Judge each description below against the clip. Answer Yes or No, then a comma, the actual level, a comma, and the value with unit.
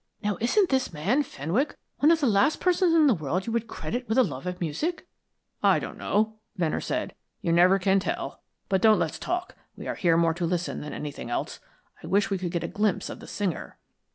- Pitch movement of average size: No, wide, 7.2 semitones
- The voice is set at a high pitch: Yes, high, 200 Hz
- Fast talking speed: Yes, fast, 225 wpm